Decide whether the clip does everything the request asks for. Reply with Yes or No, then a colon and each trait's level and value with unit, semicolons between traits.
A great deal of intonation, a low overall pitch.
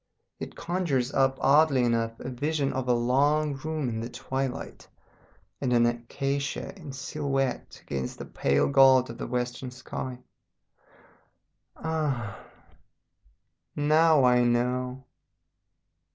No: average, 2.8 semitones; low, 130 Hz